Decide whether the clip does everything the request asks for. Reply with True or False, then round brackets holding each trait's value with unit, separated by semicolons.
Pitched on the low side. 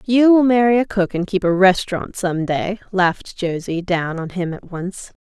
False (190 Hz)